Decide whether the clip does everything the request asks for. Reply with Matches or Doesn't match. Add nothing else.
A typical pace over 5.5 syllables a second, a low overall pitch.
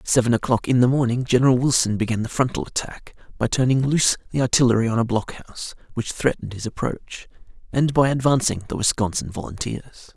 Matches